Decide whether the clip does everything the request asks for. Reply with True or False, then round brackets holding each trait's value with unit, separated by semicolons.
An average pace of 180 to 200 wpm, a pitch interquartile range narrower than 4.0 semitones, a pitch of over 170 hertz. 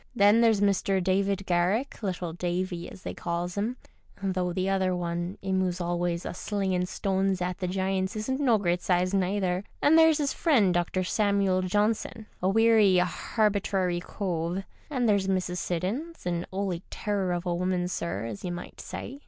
False (170 wpm; 2.4 semitones; 190 Hz)